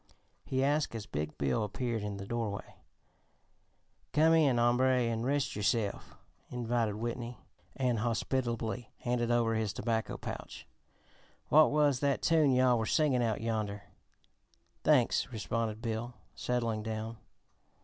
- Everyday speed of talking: No, slow, 130 wpm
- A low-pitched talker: Yes, low, 120 Hz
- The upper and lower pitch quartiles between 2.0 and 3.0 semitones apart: Yes, narrow, 2.6 semitones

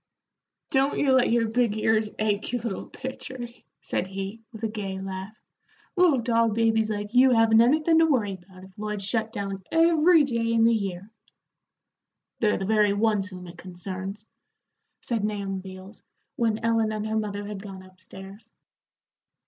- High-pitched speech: Yes, high, 215 Hz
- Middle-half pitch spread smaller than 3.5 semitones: Yes, average, 2.9 semitones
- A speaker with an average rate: Yes, average, 165 wpm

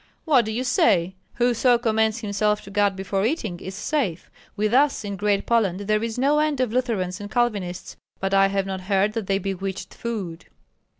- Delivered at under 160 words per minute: No, average, 190 wpm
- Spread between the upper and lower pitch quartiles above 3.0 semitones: Yes, average, 3.4 semitones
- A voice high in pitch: Yes, high, 210 Hz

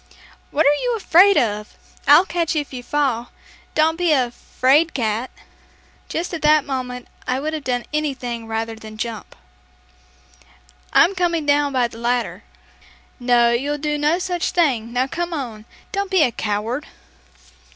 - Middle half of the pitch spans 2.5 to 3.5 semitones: No, average, 5.1 semitones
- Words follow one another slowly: No, average, 155 wpm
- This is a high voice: Yes, very high, 275 Hz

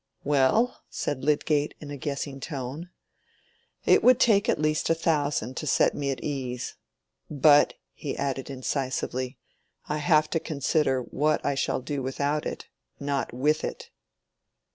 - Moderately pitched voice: Yes, medium, 145 Hz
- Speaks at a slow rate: No, average, 145 wpm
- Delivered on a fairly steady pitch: Yes, narrow, 2.3 semitones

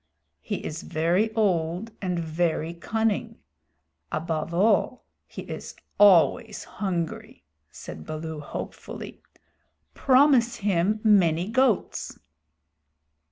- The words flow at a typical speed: No, slow, 90 wpm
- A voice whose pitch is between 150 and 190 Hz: Yes, medium, 185 Hz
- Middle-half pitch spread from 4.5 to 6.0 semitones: Yes, average, 5.1 semitones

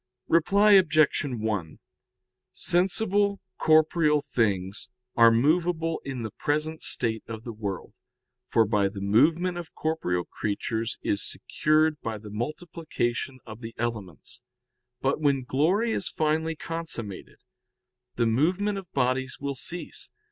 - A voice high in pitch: No, medium, 140 Hz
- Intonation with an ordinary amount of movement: No, wide, 6.5 semitones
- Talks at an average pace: No, slow, 125 wpm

